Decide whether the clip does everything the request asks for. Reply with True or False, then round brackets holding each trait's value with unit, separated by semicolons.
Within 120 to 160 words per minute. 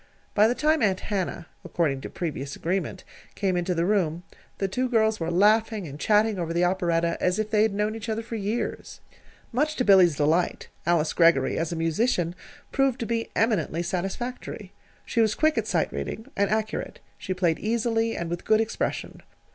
False (185 wpm)